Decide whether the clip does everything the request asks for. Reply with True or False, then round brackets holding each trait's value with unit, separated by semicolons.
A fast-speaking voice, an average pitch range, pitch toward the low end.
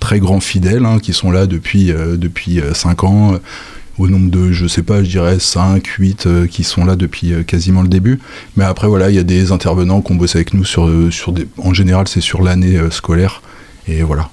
False (230 wpm; 1.8 semitones; 90 Hz)